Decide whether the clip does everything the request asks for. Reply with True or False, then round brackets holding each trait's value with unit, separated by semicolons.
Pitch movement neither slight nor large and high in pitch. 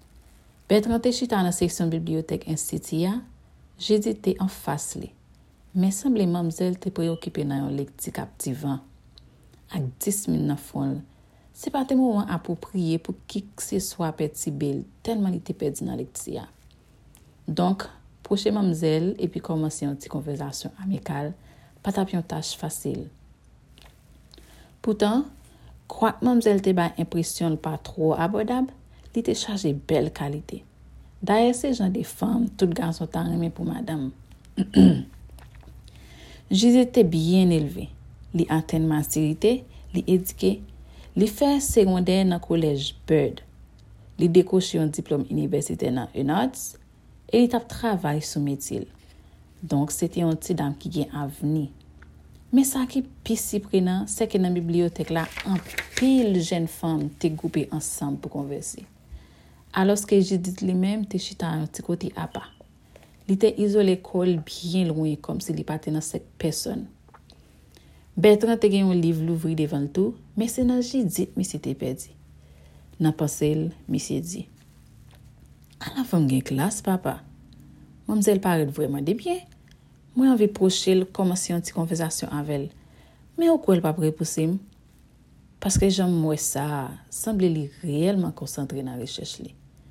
False (5.0 semitones; 170 Hz)